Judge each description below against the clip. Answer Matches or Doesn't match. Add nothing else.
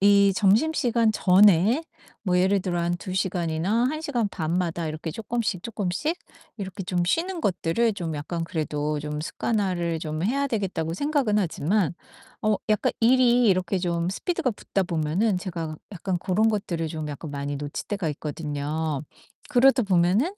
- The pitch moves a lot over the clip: Doesn't match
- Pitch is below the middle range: Doesn't match